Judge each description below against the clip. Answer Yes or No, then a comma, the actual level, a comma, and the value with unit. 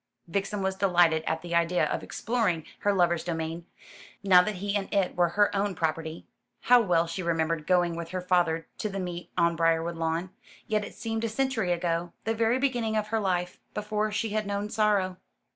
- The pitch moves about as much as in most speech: Yes, average, 3.8 semitones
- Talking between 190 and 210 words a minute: Yes, average, 195 wpm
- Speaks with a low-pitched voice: No, medium, 180 Hz